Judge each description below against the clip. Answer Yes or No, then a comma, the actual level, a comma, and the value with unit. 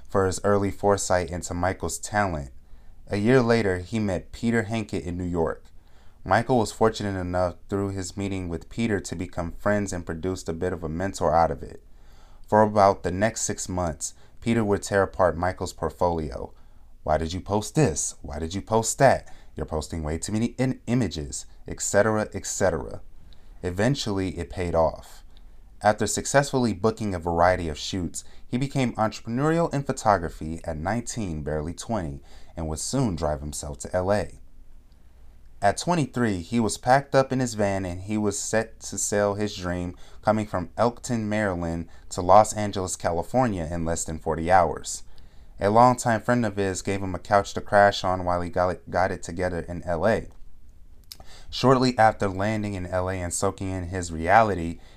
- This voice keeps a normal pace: Yes, average, 170 wpm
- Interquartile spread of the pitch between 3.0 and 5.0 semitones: Yes, average, 4.3 semitones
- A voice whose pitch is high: No, very low, 95 Hz